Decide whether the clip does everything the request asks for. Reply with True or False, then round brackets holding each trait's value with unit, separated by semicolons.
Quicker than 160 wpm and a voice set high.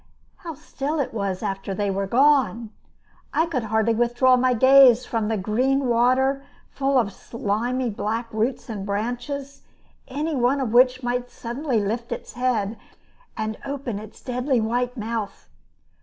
False (150 wpm; 245 Hz)